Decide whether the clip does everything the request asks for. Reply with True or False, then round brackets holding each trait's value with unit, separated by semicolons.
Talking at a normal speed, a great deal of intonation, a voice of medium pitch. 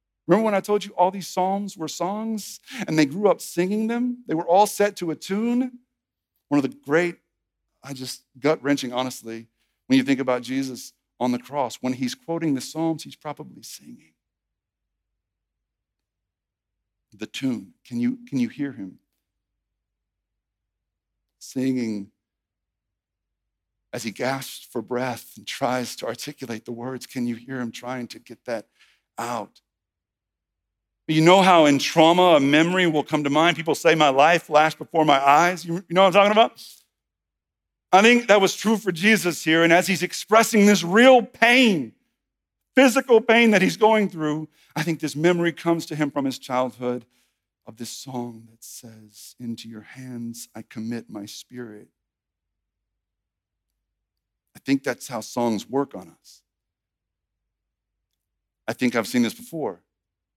False (160 wpm; 8.6 semitones; 130 Hz)